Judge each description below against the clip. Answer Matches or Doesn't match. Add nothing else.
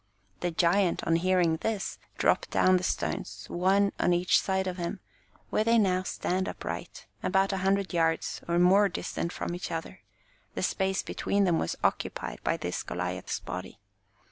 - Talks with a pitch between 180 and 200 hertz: Matches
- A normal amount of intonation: Doesn't match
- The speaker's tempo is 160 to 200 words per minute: Matches